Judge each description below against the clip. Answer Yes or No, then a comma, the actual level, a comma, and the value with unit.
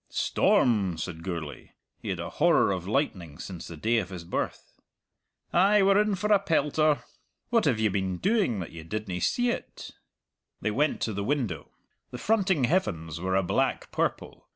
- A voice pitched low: Yes, low, 110 Hz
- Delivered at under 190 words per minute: Yes, average, 175 wpm